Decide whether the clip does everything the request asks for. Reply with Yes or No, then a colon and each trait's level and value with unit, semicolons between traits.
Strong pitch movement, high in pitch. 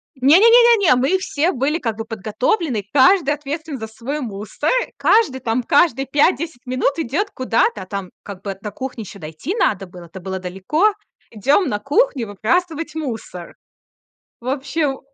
Yes: wide, 6.7 semitones; very high, 260 Hz